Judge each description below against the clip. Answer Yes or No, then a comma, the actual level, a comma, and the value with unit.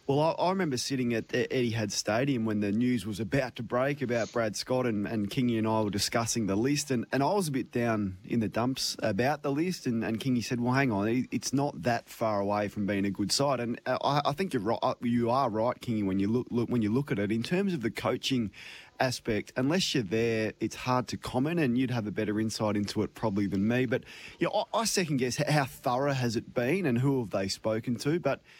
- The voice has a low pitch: Yes, low, 120 Hz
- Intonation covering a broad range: No, average, 3.6 semitones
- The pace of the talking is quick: Yes, fast, 255 wpm